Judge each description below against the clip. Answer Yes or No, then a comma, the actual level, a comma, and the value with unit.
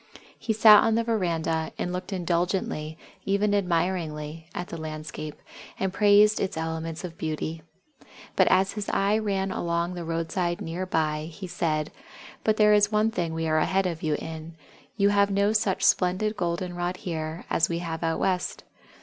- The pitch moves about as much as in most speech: Yes, average, 3.6 semitones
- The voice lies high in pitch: No, medium, 175 Hz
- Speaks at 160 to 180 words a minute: Yes, average, 175 wpm